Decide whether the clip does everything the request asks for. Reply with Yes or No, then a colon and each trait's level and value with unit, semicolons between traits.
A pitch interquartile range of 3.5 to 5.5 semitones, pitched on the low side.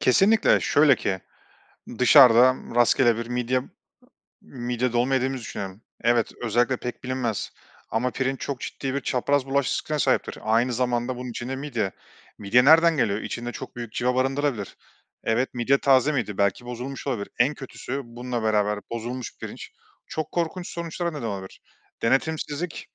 No: average, 2.7 semitones; low, 125 Hz